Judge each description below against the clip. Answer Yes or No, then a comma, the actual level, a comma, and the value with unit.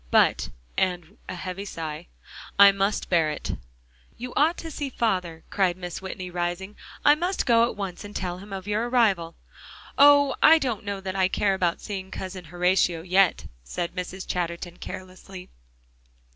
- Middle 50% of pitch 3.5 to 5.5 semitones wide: No, average, 2.9 semitones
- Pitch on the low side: No, high, 190 Hz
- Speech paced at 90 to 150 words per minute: No, average, 165 wpm